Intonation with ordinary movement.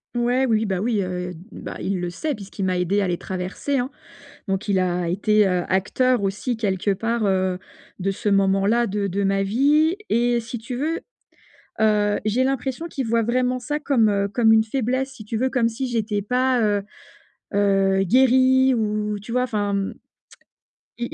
Yes: average, 4.1 semitones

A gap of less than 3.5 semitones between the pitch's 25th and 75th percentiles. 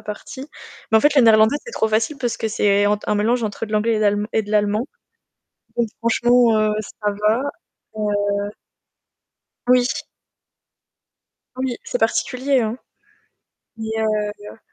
Yes: narrow, 2.5 semitones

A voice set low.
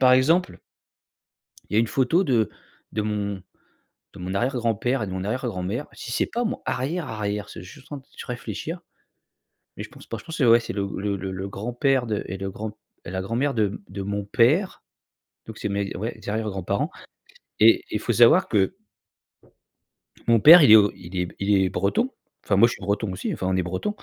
Yes: low, 110 Hz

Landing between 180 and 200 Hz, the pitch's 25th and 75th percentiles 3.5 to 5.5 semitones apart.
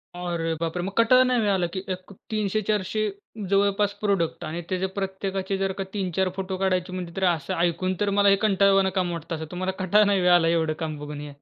No: high, 190 Hz; narrow, 2.4 semitones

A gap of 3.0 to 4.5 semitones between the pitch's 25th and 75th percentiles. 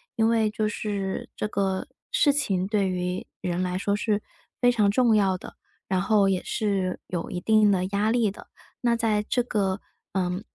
No: narrow, 2.5 semitones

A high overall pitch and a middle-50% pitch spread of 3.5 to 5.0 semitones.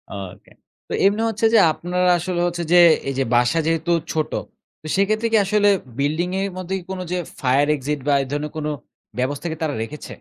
No: medium, 165 Hz; average, 4.5 semitones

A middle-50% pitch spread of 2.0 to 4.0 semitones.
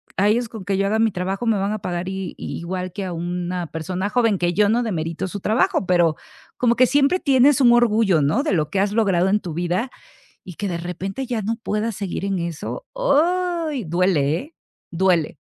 No: average, 4.8 semitones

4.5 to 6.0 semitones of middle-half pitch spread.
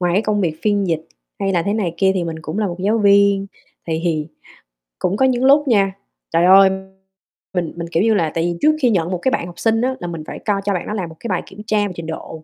No: average, 3.7 semitones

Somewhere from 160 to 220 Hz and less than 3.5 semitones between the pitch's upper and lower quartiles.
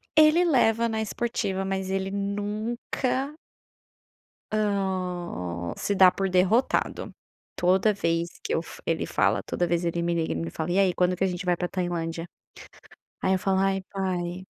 Yes: high, 190 Hz; average, 2.8 semitones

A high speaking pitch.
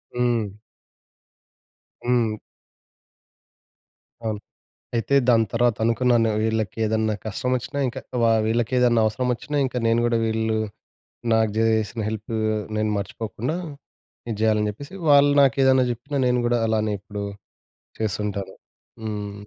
No: low, 115 Hz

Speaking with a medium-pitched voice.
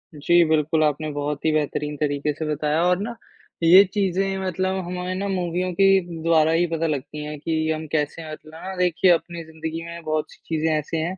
Yes: medium, 160 Hz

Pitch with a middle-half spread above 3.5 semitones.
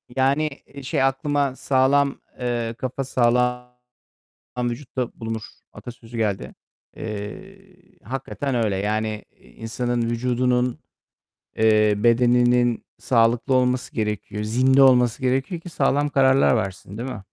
No: average, 2.8 semitones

